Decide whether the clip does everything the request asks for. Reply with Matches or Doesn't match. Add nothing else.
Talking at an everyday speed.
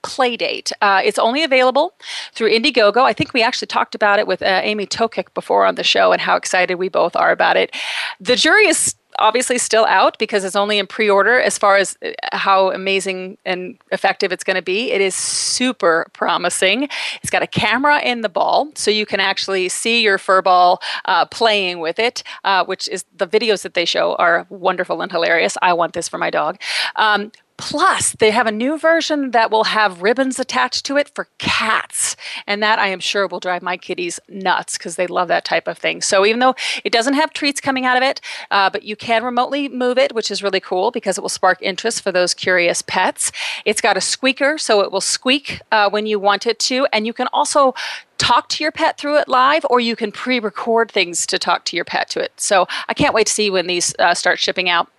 Doesn't match